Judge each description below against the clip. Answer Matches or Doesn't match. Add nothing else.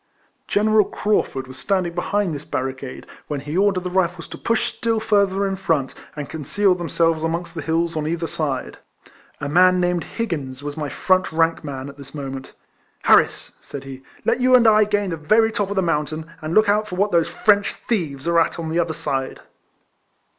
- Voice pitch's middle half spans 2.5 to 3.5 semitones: Doesn't match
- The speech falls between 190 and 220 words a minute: Matches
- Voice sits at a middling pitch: Matches